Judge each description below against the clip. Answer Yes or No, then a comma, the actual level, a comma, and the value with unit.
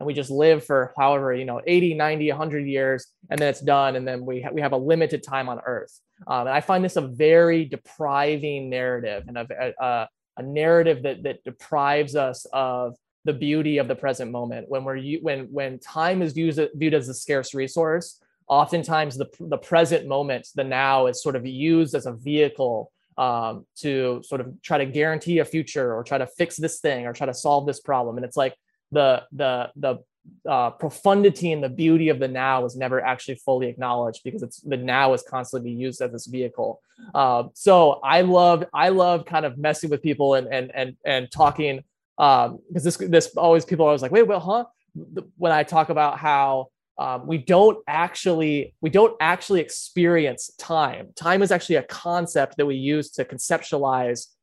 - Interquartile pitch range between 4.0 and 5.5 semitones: No, average, 3.6 semitones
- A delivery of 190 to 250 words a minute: Yes, average, 200 wpm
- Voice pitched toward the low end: No, medium, 145 Hz